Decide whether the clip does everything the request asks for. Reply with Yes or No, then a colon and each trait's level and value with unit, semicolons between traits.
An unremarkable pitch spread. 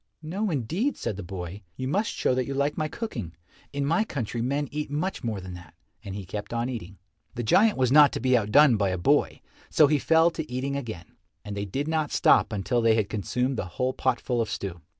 No: wide, 6.3 semitones